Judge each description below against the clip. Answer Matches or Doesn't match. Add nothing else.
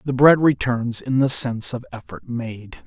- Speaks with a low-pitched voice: Matches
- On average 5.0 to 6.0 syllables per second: Doesn't match